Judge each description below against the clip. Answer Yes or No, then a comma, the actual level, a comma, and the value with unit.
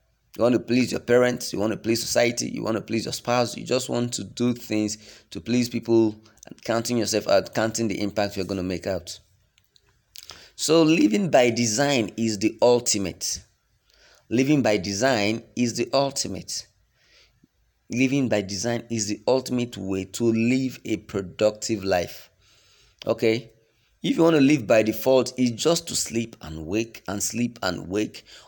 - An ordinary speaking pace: Yes, average, 170 wpm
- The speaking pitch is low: Yes, low, 115 Hz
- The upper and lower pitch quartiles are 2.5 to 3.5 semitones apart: Yes, average, 2.9 semitones